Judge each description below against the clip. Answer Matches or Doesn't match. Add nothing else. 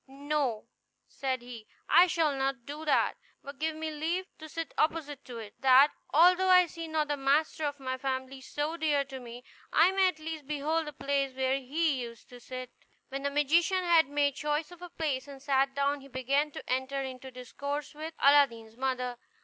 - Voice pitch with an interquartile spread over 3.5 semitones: Doesn't match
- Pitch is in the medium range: Doesn't match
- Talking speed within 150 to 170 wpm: Doesn't match